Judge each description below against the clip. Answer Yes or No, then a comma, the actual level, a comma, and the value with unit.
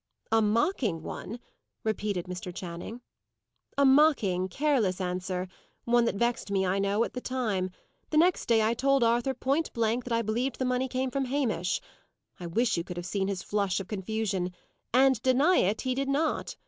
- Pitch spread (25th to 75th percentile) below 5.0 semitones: No, average, 5.3 semitones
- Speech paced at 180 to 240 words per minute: Yes, average, 185 wpm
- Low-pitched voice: No, high, 225 Hz